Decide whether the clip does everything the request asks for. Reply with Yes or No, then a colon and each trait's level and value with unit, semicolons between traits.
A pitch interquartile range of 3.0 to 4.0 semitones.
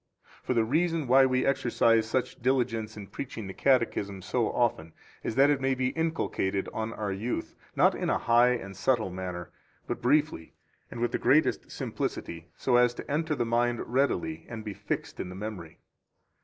No: average, 4.8 semitones